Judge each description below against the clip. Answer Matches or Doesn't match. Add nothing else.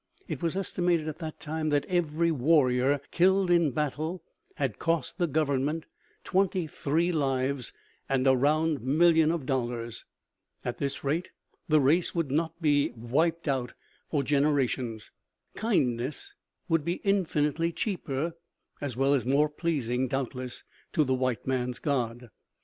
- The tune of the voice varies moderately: Matches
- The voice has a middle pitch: Matches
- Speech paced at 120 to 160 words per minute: Matches